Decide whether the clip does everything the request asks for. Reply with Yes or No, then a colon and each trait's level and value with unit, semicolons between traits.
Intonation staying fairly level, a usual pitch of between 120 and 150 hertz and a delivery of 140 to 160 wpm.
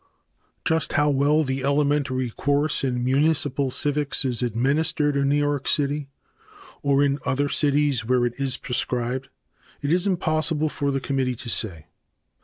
Yes: narrow, 2.2 semitones; medium, 140 Hz; average, 150 wpm